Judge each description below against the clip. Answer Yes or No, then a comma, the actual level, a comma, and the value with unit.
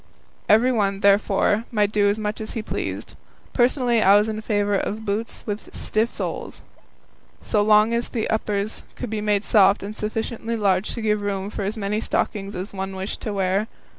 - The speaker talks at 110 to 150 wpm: No, average, 175 wpm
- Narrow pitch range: Yes, narrow, 1.6 semitones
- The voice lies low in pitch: No, high, 210 Hz